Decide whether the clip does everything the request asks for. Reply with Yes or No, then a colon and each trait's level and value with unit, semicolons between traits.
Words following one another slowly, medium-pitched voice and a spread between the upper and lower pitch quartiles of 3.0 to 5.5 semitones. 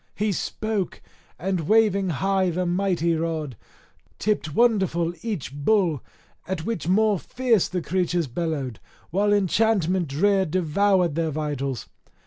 Yes: slow, 120 wpm; medium, 180 Hz; average, 4.0 semitones